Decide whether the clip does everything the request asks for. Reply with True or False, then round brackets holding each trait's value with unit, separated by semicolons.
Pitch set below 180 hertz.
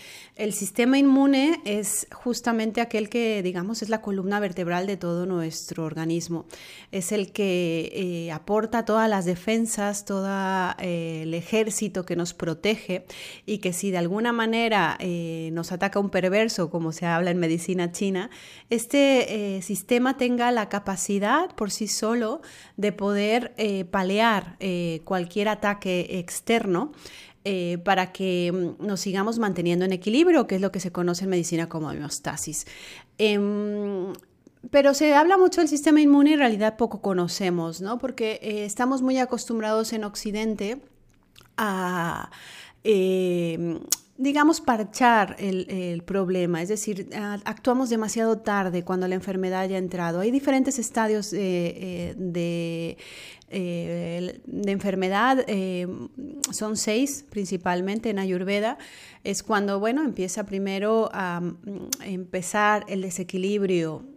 False (200 Hz)